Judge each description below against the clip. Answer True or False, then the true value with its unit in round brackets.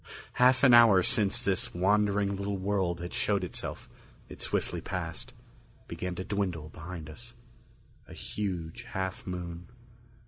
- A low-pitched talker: True (95 Hz)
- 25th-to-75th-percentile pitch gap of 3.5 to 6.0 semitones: False (2.9 semitones)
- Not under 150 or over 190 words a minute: False (135 wpm)